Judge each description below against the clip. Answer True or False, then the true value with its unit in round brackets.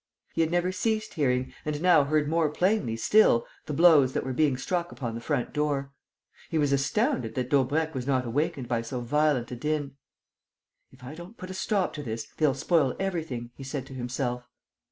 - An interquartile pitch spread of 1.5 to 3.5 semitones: False (4.4 semitones)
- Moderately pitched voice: True (145 Hz)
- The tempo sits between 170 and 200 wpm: True (195 wpm)